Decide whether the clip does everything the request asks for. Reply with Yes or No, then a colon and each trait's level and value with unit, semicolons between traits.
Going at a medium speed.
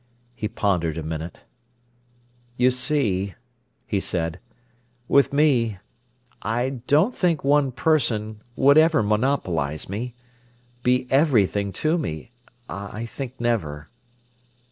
No: slow, 95 wpm